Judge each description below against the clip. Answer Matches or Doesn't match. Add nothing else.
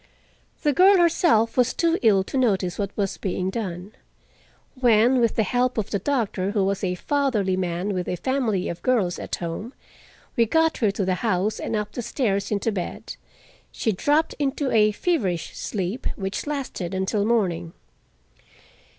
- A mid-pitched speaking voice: Doesn't match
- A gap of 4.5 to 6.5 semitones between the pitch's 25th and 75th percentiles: Matches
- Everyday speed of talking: Matches